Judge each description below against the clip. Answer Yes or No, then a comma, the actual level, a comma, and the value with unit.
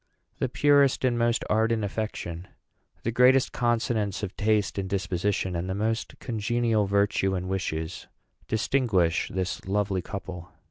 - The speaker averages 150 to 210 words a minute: No, slow, 135 wpm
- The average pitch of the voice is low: Yes, low, 105 Hz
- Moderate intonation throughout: Yes, average, 3.7 semitones